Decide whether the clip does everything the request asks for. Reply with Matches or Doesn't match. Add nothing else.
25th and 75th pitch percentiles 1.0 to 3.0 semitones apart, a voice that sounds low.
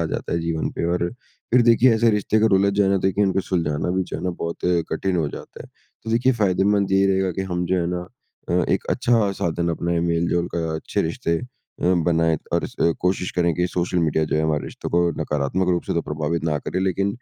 Matches